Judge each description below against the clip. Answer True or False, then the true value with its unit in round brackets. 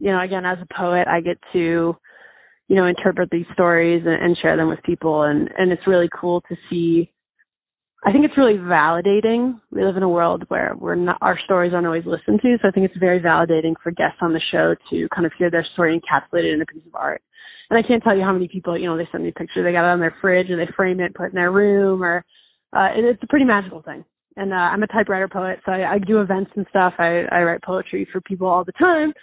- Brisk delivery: True (265 wpm)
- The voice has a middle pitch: True (180 Hz)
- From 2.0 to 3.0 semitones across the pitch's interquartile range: True (2.4 semitones)